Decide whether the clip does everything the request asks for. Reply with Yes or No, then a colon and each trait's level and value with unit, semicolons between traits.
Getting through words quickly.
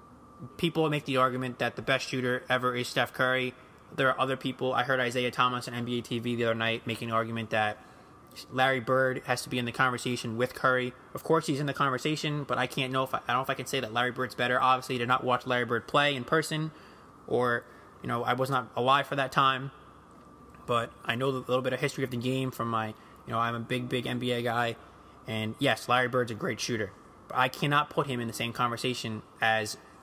Yes: fast, 240 wpm